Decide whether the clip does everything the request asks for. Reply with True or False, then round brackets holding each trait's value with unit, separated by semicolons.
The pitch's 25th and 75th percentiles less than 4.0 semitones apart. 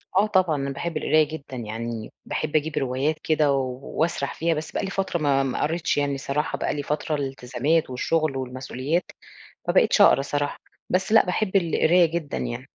True (3.5 semitones)